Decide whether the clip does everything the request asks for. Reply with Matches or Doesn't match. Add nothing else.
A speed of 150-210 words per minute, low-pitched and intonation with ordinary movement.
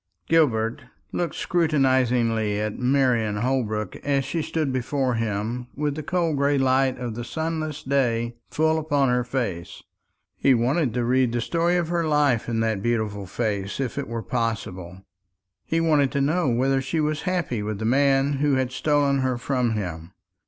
Matches